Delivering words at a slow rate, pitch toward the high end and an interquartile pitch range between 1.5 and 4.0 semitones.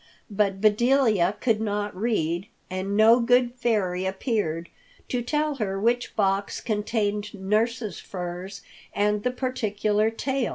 Yes: slow, 125 wpm; high, 210 Hz; average, 3.5 semitones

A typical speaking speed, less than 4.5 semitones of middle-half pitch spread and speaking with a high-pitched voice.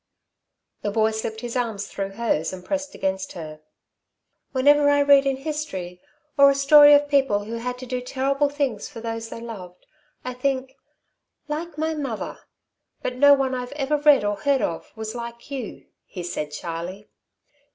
No: average, 170 wpm; wide, 5.4 semitones; very high, 250 Hz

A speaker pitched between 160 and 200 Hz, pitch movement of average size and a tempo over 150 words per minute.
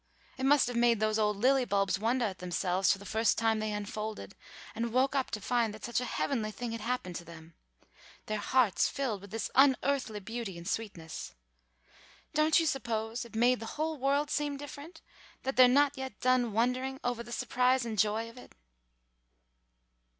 No: high, 235 Hz; average, 3.6 semitones; average, 185 wpm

